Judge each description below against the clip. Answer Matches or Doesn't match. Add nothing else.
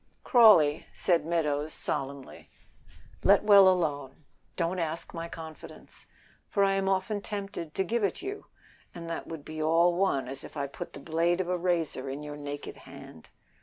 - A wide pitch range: Doesn't match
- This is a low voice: Doesn't match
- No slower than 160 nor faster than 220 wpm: Matches